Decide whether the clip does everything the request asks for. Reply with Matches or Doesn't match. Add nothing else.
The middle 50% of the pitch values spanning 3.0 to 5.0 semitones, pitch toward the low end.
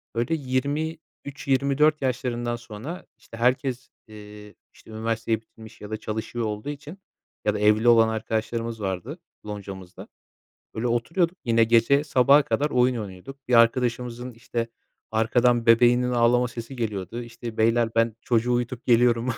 Doesn't match